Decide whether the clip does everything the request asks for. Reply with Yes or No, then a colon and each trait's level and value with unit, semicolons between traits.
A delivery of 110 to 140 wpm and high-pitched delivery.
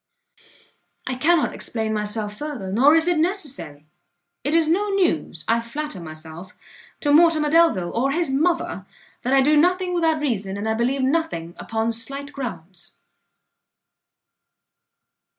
Yes: slow, 135 wpm; very high, 270 Hz